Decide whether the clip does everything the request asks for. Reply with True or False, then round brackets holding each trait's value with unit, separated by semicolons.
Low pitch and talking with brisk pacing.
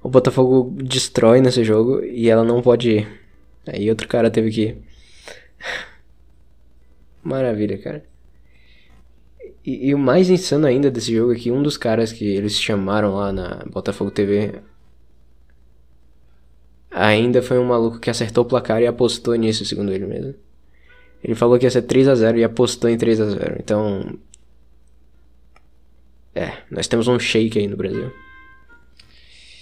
False (105 Hz; 150 wpm)